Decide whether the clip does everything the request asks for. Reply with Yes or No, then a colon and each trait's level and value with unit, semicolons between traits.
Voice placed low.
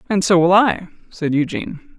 No: medium, 180 Hz